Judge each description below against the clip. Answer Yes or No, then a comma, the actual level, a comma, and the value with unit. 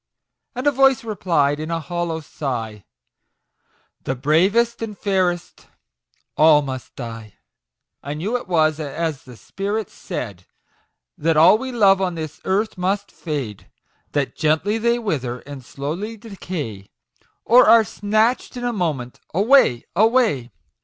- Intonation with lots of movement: Yes, wide, 7.2 semitones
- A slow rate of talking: No, average, 145 wpm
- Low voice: No, medium, 170 Hz